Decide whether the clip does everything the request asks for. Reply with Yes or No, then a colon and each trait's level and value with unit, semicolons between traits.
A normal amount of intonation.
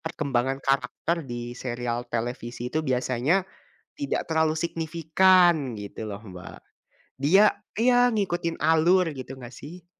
No: wide, 6.0 semitones